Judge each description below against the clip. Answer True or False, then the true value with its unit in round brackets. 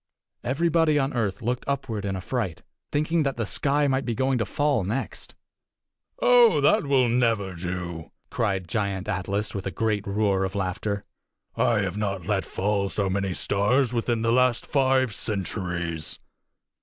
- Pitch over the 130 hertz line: False (110 Hz)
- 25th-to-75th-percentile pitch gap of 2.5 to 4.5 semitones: False (5.2 semitones)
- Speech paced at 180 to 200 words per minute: False (155 wpm)